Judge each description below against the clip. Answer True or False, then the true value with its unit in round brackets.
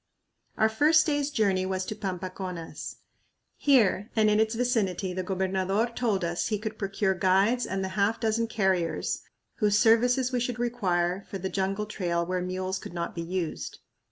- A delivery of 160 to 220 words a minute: True (170 wpm)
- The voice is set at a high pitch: True (195 Hz)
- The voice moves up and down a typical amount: True (3.3 semitones)